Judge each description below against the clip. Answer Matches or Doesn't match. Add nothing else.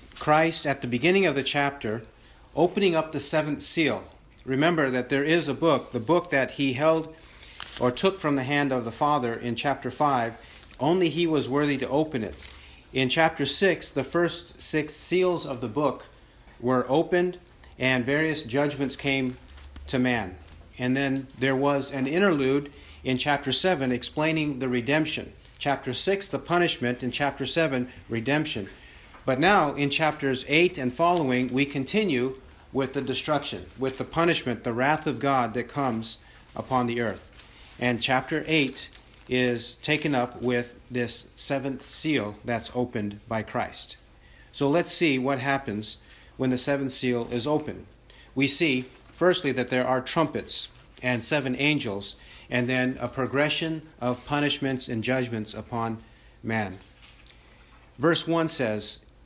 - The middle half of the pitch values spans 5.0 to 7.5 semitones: Doesn't match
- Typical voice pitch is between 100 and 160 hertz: Matches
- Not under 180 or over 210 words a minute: Doesn't match